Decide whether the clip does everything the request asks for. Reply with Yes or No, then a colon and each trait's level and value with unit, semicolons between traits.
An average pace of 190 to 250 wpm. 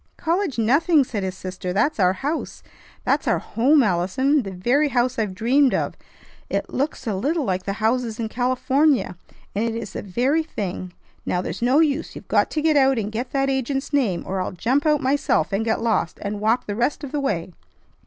Yes: fast, 205 wpm